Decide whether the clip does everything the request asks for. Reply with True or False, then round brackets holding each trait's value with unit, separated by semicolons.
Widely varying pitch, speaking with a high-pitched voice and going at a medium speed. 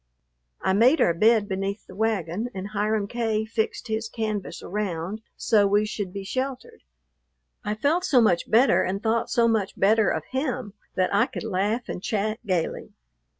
False (2.6 semitones; 215 Hz; 170 wpm)